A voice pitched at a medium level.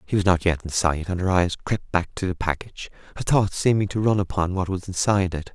No: very low, 90 Hz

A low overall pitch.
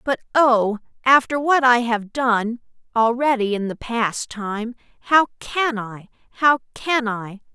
No: high, 240 Hz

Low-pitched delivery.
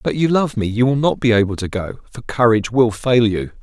Yes: low, 115 Hz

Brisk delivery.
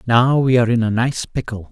Yes: fast, 245 wpm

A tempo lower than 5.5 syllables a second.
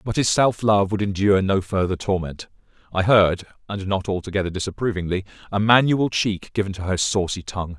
No: 5.6 syllables/s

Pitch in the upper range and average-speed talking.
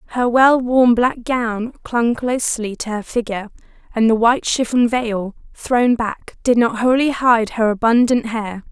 Yes: high, 235 Hz; average, 165 wpm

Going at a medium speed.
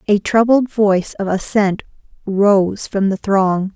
Yes: average, 145 wpm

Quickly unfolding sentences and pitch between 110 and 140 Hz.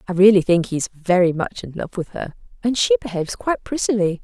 No: fast, 225 wpm; high, 195 Hz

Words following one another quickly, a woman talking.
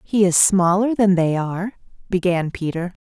No: average, 160 wpm; female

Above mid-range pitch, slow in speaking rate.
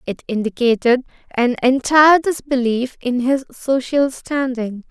Yes: very high, 255 Hz; slow, 110 wpm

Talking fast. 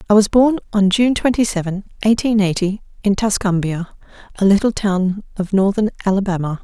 No: average, 155 wpm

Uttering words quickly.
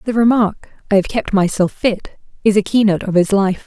Yes: fast, 215 wpm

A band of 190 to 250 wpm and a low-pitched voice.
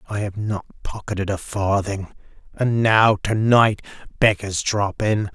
No: average, 145 wpm; low, 105 Hz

